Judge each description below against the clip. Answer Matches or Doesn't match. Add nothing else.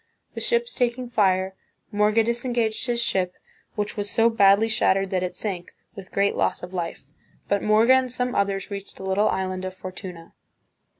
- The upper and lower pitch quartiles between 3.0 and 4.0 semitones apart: Matches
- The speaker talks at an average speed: Matches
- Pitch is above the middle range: Matches